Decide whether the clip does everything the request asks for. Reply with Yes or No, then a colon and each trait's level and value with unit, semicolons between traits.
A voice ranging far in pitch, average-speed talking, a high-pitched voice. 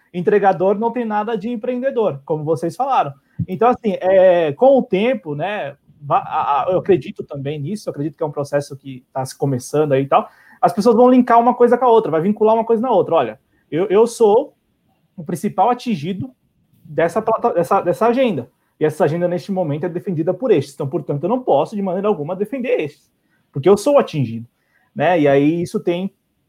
No: wide, 6.8 semitones; fast, 200 wpm; high, 195 Hz